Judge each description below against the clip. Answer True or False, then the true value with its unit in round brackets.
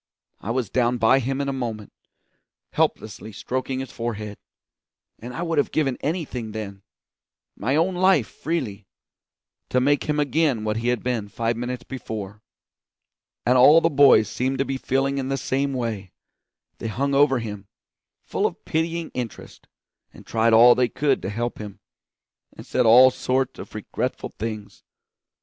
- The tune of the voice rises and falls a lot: False (3.6 semitones)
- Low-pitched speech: True (125 Hz)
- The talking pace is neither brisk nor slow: True (165 wpm)